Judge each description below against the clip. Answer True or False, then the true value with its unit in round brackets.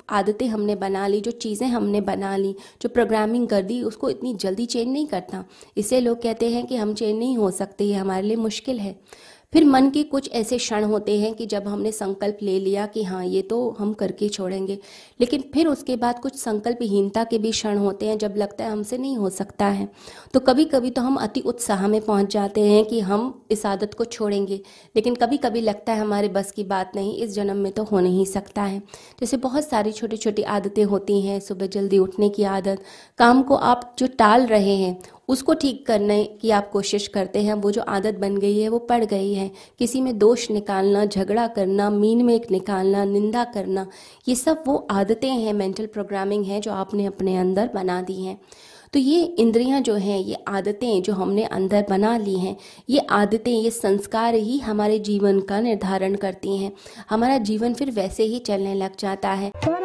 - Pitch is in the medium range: False (210 Hz)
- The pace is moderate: False (205 wpm)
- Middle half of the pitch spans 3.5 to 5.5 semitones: False (2.8 semitones)